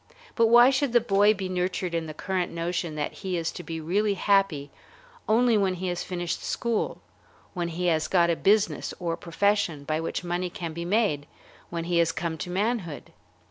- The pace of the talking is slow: No, average, 195 wpm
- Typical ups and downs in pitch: Yes, average, 3.4 semitones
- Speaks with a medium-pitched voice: Yes, medium, 180 Hz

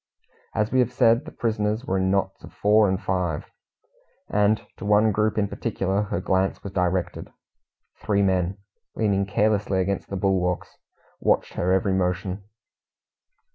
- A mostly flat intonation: Yes, narrow, 2.2 semitones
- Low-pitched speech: Yes, low, 100 Hz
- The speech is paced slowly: No, average, 150 wpm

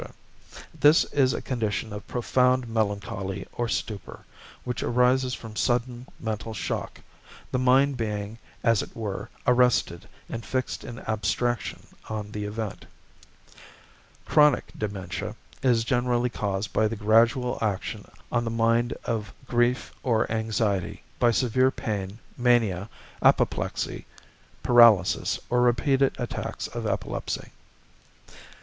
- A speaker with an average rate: No, slow, 120 wpm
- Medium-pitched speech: No, low, 115 Hz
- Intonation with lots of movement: No, average, 2.8 semitones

